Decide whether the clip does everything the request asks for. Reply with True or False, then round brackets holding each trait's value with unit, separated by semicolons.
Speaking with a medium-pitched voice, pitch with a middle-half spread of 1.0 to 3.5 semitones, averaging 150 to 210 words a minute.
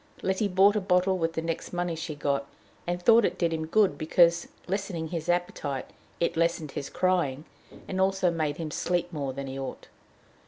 True (170 Hz; 2.9 semitones; 190 wpm)